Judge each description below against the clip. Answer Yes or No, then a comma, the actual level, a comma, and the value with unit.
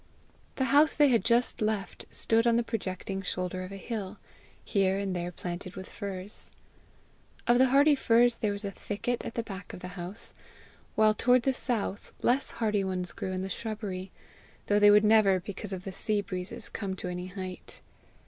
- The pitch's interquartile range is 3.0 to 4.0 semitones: Yes, average, 3.5 semitones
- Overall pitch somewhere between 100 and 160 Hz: No, high, 200 Hz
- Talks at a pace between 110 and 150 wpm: No, average, 190 wpm